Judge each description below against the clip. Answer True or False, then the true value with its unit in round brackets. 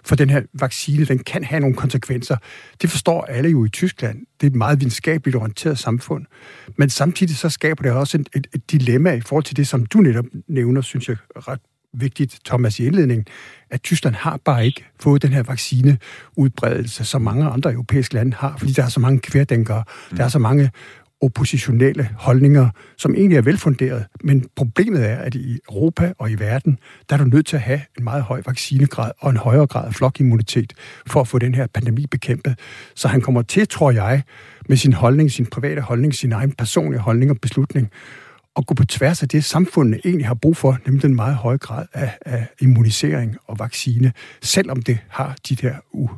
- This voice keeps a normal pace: True (200 wpm)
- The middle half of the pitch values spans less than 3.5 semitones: True (2.9 semitones)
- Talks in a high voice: False (135 Hz)